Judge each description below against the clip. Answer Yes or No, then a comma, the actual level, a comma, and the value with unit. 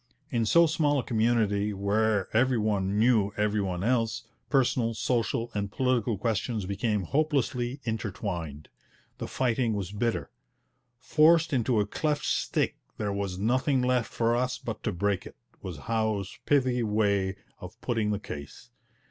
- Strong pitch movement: No, average, 3.6 semitones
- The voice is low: Yes, low, 110 Hz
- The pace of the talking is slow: No, average, 150 wpm